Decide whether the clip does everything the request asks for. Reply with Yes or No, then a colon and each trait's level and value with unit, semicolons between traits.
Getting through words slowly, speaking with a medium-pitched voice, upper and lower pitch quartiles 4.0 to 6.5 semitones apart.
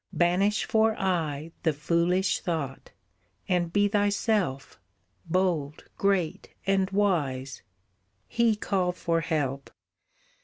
Yes: slow, 100 wpm; medium, 180 Hz; average, 4.3 semitones